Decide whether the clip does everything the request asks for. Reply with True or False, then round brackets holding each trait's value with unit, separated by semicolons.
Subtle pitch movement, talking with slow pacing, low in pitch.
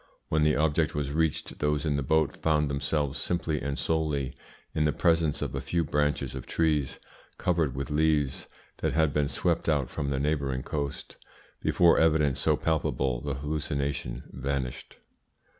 False (2.2 semitones; 160 wpm; 75 Hz)